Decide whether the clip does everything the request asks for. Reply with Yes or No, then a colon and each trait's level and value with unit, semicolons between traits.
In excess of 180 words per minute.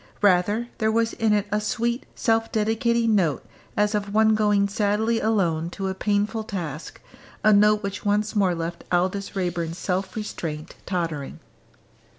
No: average, 155 wpm